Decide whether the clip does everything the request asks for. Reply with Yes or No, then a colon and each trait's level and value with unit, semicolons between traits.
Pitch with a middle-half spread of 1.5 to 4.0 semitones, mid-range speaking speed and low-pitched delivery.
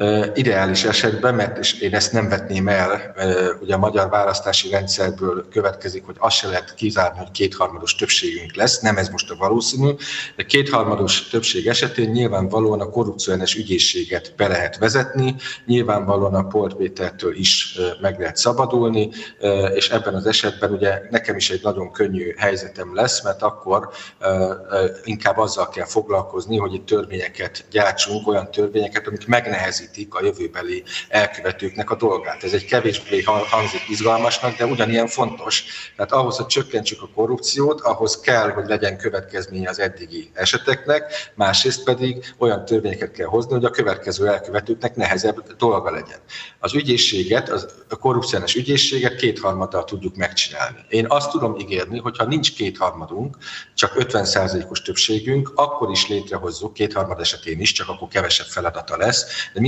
No: average, 4.5 semitones; average, 145 wpm; low, 110 Hz